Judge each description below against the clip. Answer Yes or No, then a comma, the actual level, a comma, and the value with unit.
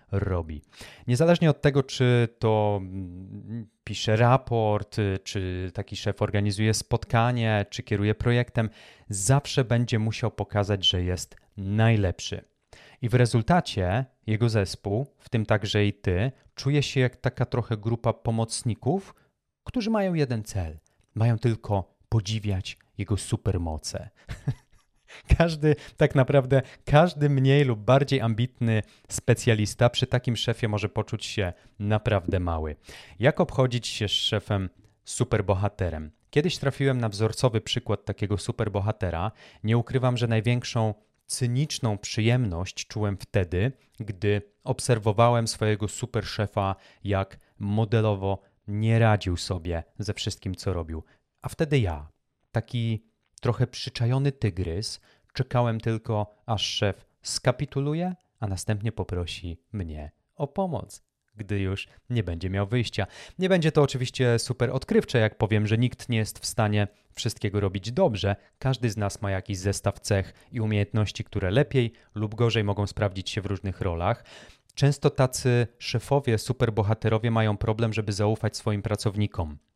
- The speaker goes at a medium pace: Yes, average, 130 wpm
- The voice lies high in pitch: No, low, 110 Hz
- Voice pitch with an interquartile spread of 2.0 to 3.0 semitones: No, average, 3.4 semitones